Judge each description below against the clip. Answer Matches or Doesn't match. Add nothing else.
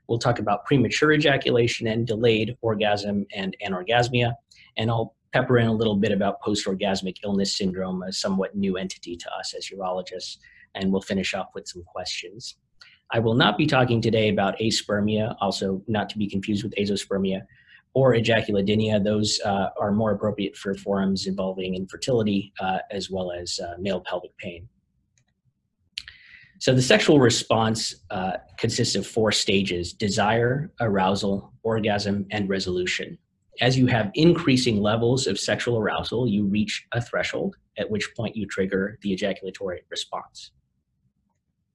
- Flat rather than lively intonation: Doesn't match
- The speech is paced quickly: Doesn't match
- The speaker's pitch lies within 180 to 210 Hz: Doesn't match